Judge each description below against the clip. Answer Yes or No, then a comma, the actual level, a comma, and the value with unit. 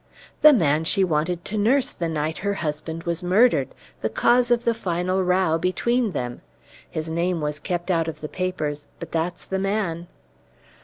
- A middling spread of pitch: Yes, average, 3.4 semitones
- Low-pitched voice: No, medium, 175 Hz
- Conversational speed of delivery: Yes, average, 175 wpm